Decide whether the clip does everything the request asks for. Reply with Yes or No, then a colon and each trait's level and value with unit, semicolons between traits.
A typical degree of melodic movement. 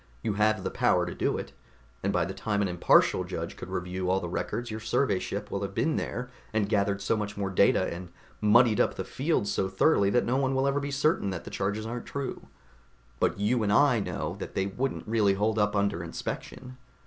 Yes: average, 3.8 semitones